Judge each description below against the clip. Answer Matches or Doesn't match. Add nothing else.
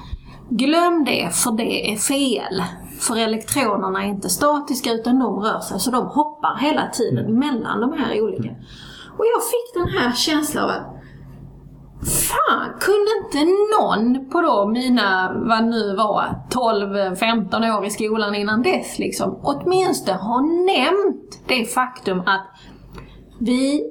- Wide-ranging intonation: Matches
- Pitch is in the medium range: Doesn't match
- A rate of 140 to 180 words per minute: Matches